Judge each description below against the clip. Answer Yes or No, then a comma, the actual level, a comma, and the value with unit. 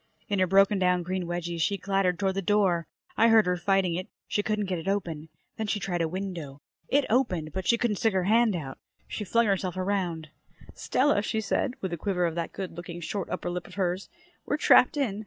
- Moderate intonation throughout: Yes, average, 3.0 semitones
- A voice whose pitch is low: No, high, 190 Hz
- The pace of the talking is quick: Yes, fast, 225 wpm